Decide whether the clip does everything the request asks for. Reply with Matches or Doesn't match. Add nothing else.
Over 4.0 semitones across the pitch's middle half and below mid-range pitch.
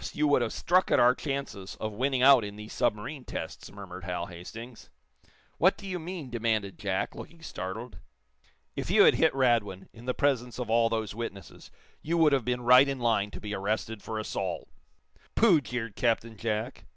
Matches